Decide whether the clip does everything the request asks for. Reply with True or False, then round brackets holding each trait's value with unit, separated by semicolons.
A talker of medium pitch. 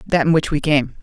True (150 Hz)